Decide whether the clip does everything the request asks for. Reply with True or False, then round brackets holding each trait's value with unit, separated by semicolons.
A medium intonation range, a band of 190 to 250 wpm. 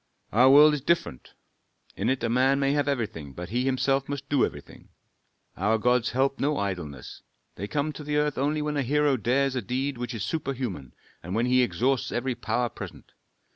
True (3.4 semitones; 195 wpm)